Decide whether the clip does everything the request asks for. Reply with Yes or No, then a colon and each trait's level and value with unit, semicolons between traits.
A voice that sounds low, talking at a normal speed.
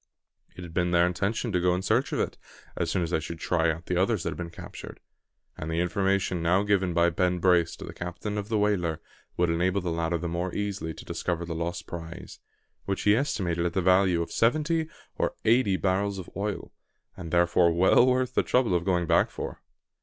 No: very low, 90 Hz; fast, 220 wpm